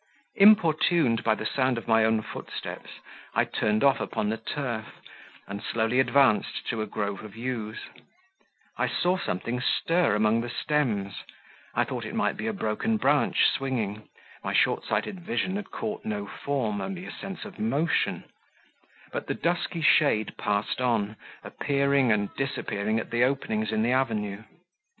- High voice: No, low, 120 Hz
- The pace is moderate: Yes, average, 160 wpm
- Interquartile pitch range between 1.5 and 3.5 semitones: No, average, 5.2 semitones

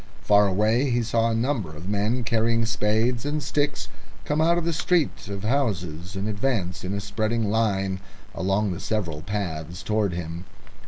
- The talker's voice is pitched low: Yes, low, 105 Hz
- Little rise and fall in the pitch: No, average, 3.7 semitones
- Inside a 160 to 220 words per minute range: Yes, average, 170 wpm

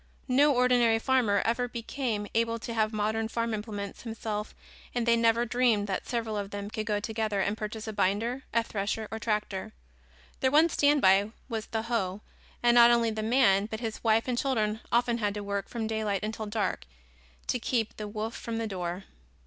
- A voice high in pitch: Yes, high, 220 Hz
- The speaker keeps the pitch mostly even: Yes, narrow, 2.1 semitones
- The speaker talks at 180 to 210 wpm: Yes, average, 190 wpm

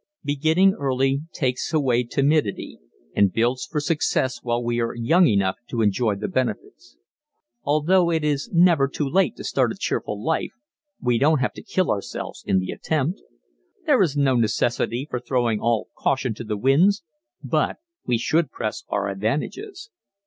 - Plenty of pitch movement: No, average, 4.9 semitones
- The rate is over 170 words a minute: No, average, 165 wpm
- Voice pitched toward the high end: No, low, 130 Hz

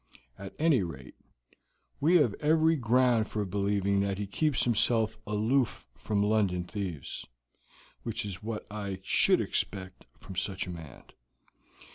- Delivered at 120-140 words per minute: Yes, slow, 135 wpm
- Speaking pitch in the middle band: No, low, 105 Hz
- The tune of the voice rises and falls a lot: No, average, 3.7 semitones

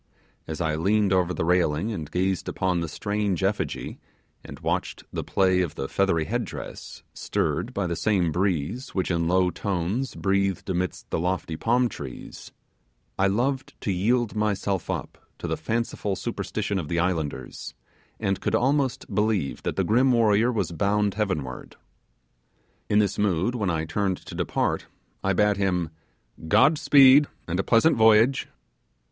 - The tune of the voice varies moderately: Yes, average, 3.6 semitones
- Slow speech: No, average, 160 wpm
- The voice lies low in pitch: Yes, very low, 95 Hz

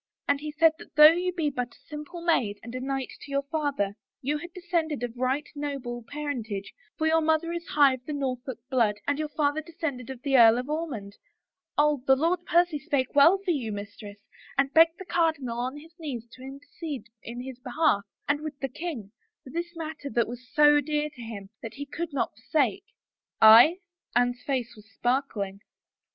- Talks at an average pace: No, fast, 210 wpm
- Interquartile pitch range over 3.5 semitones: Yes, average, 4.3 semitones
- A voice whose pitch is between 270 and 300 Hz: Yes, very high, 280 Hz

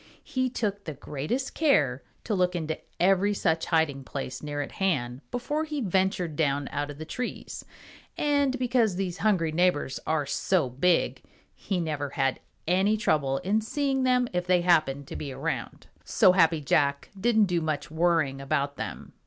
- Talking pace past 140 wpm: Yes, average, 170 wpm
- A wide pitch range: Yes, wide, 6.1 semitones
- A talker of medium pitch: Yes, medium, 175 Hz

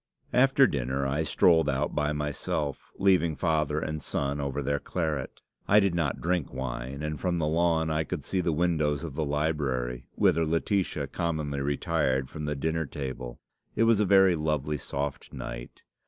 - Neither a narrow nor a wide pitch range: Yes, average, 3.2 semitones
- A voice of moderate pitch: No, very low, 75 Hz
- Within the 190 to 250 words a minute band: No, average, 170 wpm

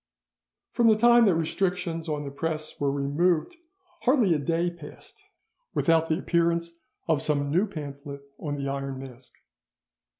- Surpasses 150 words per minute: No, average, 145 wpm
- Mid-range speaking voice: Yes, medium, 160 Hz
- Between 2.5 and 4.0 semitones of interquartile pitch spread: Yes, average, 3.6 semitones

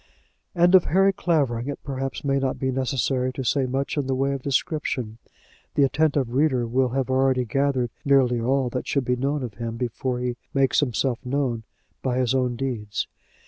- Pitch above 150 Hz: No, low, 130 Hz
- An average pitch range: No, narrow, 2.0 semitones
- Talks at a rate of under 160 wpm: No, average, 185 wpm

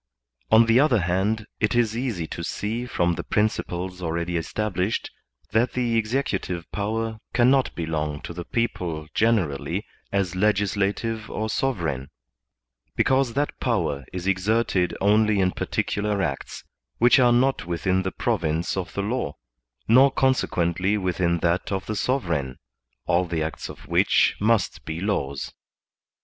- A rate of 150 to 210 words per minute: No, average, 140 wpm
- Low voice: Yes, low, 100 Hz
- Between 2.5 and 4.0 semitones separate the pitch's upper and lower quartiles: No, average, 4.7 semitones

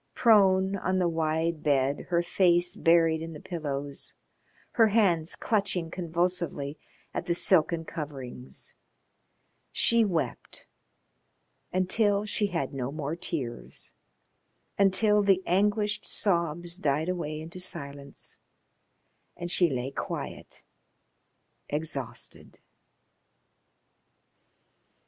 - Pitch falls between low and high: Yes, medium, 170 Hz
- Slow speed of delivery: Yes, slow, 95 wpm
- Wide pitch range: No, average, 3.8 semitones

